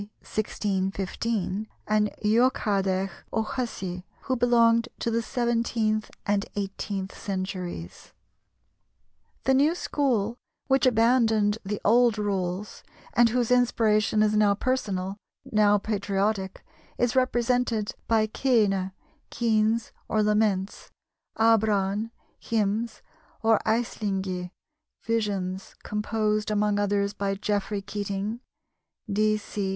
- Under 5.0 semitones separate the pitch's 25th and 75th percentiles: Yes, narrow, 2.5 semitones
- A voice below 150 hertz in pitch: No, high, 215 Hz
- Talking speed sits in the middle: No, slow, 95 wpm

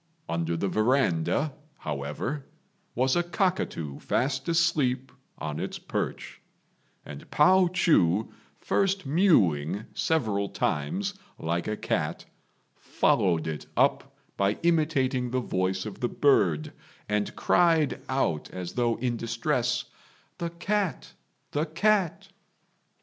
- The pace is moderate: No, slow, 110 wpm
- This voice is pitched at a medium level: No, low, 125 Hz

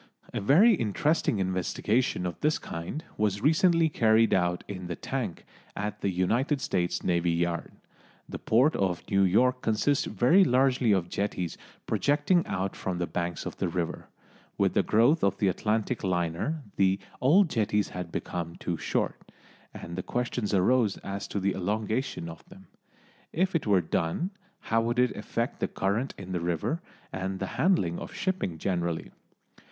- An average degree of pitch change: No, wide, 6.3 semitones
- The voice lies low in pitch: Yes, low, 100 Hz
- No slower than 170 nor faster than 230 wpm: No, average, 160 wpm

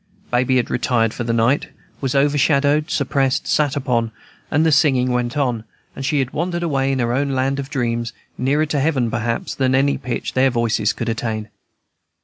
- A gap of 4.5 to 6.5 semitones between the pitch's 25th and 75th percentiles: No, average, 3.0 semitones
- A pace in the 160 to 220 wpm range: Yes, average, 180 wpm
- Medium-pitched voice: No, low, 130 Hz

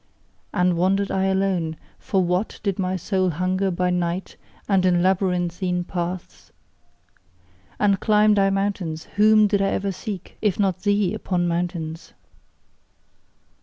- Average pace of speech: No, slow, 130 wpm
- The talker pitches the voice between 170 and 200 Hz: Yes, medium, 185 Hz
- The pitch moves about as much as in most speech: No, narrow, 1.9 semitones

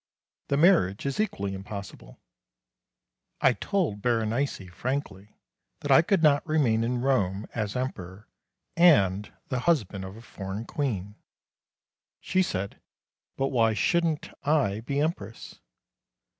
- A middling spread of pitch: No, wide, 6.4 semitones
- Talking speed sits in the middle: No, slow, 120 wpm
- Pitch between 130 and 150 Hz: No, low, 120 Hz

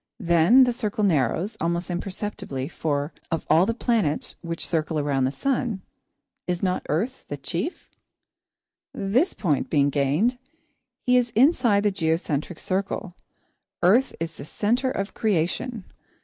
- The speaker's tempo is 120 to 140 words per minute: Yes, slow, 135 wpm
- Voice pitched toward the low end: No, medium, 185 Hz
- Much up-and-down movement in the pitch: Yes, wide, 6.3 semitones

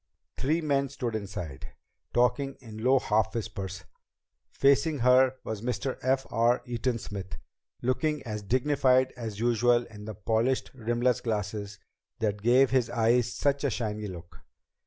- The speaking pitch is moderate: No, low, 120 Hz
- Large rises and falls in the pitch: No, average, 3.3 semitones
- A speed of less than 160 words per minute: Yes, average, 140 wpm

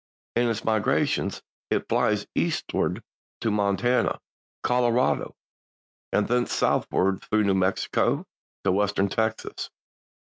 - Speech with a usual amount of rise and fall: Yes, average, 3.1 semitones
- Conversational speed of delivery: No, slow, 105 wpm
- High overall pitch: No, low, 110 Hz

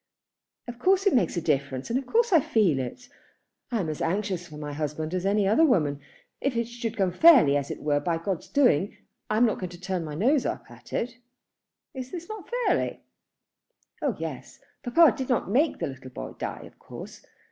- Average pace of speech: No, fast, 210 wpm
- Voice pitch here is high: Yes, high, 200 Hz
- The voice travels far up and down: Yes, wide, 8.3 semitones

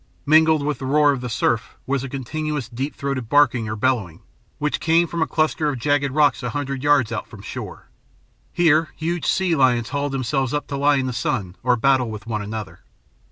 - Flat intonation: No, average, 3.4 semitones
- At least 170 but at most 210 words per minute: Yes, fast, 205 wpm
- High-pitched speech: No, low, 135 Hz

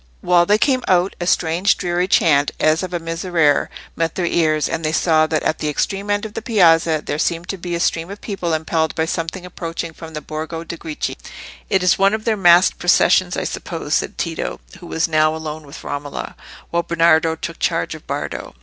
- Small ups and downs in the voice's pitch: Yes, narrow, 2.2 semitones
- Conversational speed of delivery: No, fast, 215 wpm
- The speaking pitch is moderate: Yes, medium, 165 Hz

